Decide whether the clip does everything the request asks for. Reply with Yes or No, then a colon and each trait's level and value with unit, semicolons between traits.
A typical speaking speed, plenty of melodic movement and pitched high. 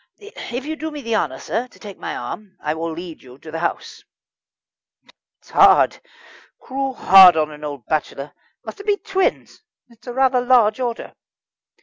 Yes: average, 180 wpm; wide, 8.6 semitones; high, 215 Hz